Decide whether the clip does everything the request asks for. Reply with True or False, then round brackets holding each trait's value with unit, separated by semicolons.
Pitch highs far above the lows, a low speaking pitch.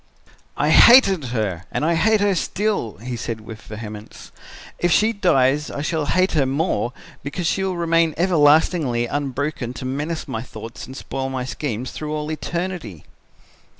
False (6.0 semitones; 145 Hz)